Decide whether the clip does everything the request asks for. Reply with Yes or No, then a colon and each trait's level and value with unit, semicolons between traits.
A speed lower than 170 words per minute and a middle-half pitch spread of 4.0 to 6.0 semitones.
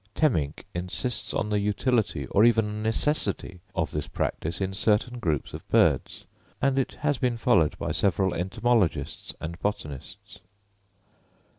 Yes: slow, 135 wpm; wide, 5.5 semitones